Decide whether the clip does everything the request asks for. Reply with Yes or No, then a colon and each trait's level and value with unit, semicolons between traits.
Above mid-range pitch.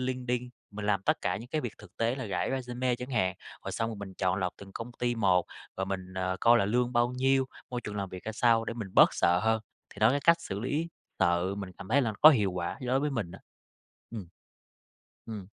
No: low, 115 Hz